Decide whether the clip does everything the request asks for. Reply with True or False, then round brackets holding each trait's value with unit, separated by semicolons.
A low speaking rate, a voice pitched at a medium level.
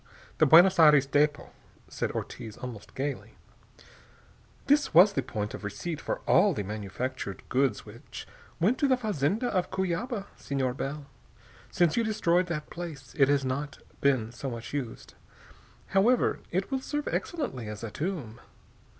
False (150 wpm; 145 Hz)